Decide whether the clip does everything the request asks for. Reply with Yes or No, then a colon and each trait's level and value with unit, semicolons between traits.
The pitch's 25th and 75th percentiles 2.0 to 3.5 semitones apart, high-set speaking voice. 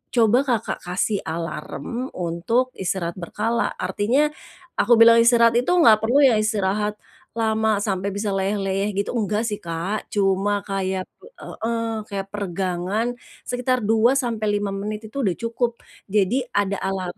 Yes: average, 3.2 semitones; high, 210 Hz